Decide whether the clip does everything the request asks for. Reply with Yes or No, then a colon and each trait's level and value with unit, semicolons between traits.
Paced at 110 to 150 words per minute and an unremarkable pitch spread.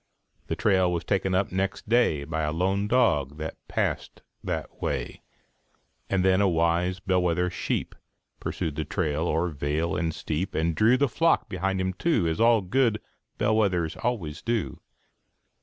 No: average, 160 wpm; average, 3.7 semitones